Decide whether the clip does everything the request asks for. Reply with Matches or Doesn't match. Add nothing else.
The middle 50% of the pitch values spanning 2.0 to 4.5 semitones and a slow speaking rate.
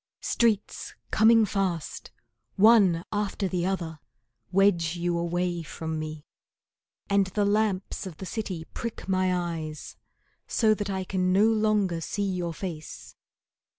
Matches